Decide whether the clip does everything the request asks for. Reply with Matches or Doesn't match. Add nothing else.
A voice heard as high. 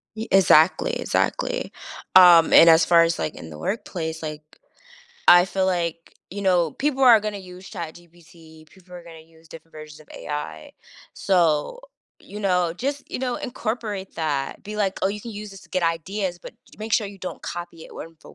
Doesn't match